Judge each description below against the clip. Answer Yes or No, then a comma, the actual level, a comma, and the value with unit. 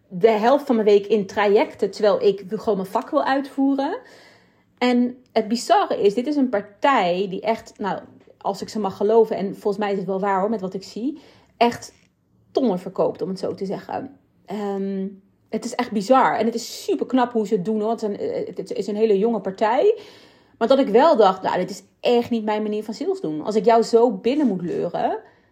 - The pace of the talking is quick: Yes, fast, 225 wpm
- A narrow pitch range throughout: No, average, 3.3 semitones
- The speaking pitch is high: Yes, high, 225 Hz